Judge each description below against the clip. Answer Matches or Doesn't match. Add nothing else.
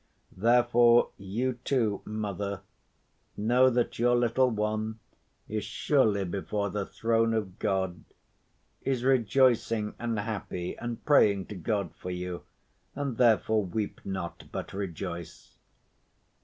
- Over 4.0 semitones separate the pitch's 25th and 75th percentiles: Doesn't match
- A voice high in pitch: Doesn't match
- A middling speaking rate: Doesn't match